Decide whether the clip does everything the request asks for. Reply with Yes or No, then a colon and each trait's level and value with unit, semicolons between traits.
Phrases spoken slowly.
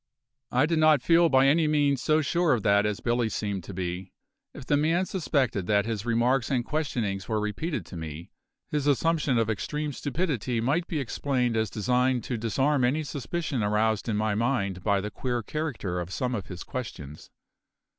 No: average, 185 wpm